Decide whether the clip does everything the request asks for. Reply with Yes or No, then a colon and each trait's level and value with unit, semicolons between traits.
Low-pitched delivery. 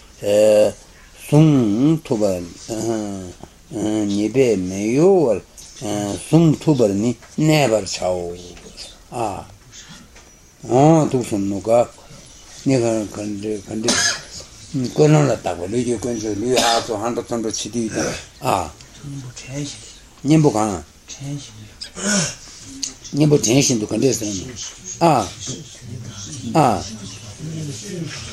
Yes: low, 115 Hz